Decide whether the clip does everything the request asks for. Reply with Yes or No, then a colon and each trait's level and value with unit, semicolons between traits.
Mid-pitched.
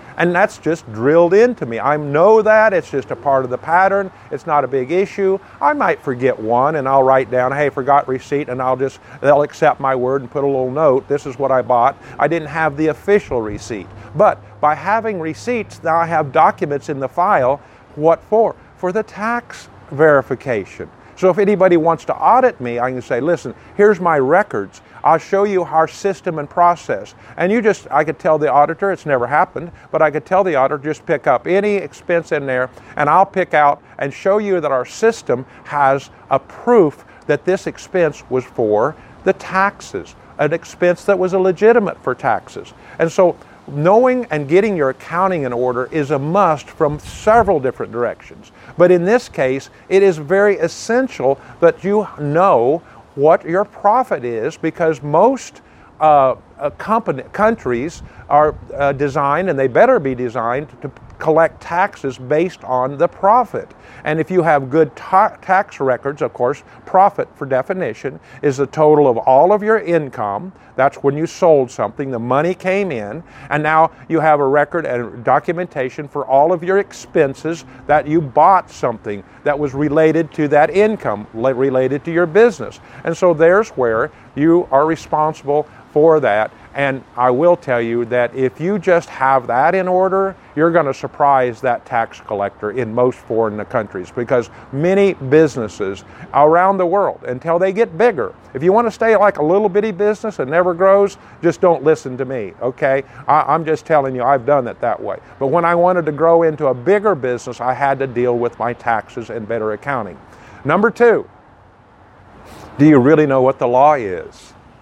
Yes: medium, 150 Hz